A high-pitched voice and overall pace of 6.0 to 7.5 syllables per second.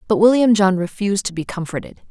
Yes: high, 200 Hz; 6.3 syllables/s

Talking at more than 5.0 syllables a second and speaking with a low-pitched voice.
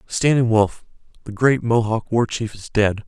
No: 4.5 syllables/s; low, 115 Hz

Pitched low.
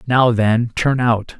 Yes: low, 120 Hz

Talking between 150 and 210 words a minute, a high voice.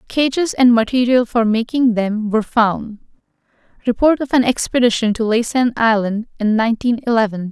No: slow, 135 wpm; high, 235 Hz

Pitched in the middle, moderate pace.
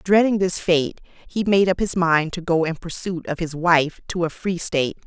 No: medium, 175 Hz; fast, 225 wpm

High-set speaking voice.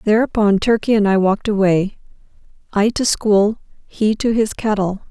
Yes: high, 210 Hz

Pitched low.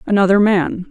No: high, 195 Hz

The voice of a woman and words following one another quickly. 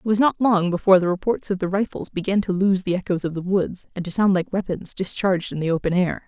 Yes: female; fast, 270 wpm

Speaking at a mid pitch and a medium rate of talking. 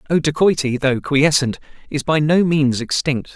Yes: medium, 145 Hz; average, 160 wpm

